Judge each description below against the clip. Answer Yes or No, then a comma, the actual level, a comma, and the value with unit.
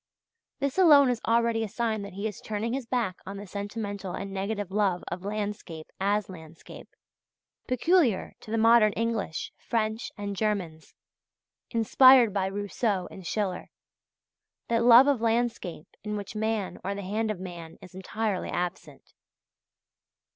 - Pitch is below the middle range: No, high, 210 Hz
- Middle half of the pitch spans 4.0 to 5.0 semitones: No, average, 3.1 semitones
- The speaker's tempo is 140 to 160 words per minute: Yes, average, 145 wpm